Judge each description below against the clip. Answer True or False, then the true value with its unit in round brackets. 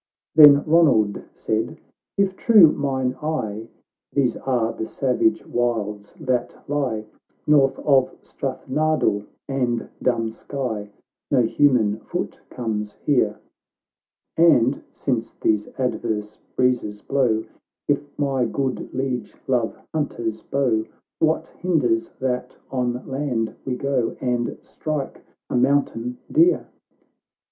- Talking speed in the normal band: False (115 wpm)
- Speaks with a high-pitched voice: False (125 Hz)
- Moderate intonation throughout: True (3.8 semitones)